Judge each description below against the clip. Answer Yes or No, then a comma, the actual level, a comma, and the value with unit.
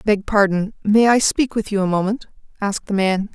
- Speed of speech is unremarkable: No, fast, 215 wpm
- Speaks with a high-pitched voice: Yes, high, 205 Hz